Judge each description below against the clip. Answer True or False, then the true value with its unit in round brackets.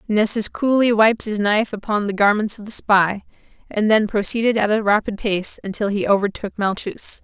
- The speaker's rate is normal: True (180 wpm)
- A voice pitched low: False (210 Hz)